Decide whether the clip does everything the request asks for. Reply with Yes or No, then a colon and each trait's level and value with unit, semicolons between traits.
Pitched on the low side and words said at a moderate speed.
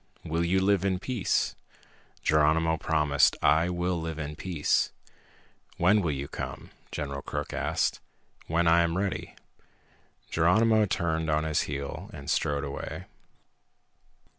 No: very low, 80 Hz; slow, 130 wpm